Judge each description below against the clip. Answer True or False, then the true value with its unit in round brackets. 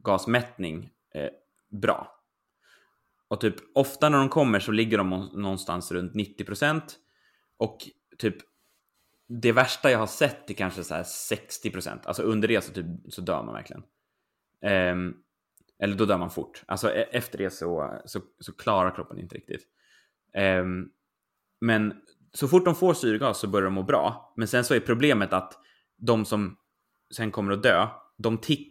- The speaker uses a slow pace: False (160 wpm)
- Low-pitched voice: True (105 Hz)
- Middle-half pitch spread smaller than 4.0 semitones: False (4.3 semitones)